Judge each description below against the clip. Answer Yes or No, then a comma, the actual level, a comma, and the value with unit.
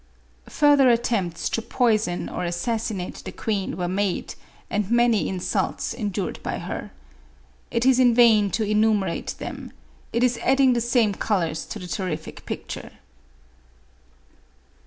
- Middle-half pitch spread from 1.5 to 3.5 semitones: No, average, 4.2 semitones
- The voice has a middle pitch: No, high, 215 Hz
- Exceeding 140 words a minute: No, slow, 135 wpm